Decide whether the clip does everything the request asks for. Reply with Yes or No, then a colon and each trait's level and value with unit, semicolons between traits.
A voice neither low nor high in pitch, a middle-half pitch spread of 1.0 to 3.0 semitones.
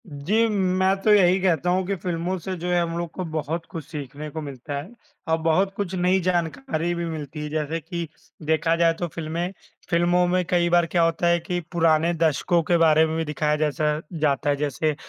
Yes: medium, 165 Hz; narrow, 2.4 semitones